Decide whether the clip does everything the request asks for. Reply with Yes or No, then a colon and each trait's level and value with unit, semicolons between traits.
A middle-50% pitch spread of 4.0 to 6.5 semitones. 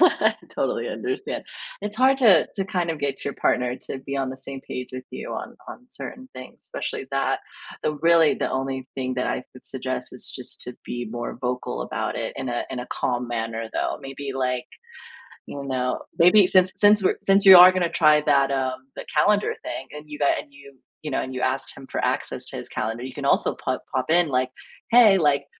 Yes: average, 5.0 semitones